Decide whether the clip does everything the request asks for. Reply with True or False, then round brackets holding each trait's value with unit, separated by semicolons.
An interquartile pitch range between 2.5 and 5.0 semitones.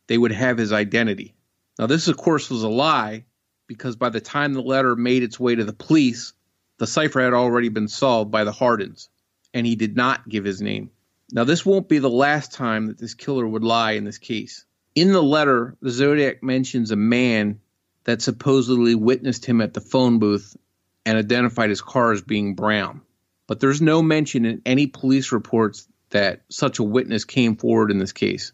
True (3.4 semitones)